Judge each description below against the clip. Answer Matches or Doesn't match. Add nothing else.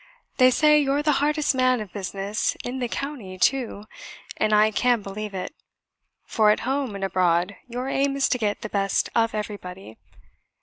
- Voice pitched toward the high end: Matches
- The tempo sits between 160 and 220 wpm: Matches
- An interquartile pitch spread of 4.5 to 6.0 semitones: Matches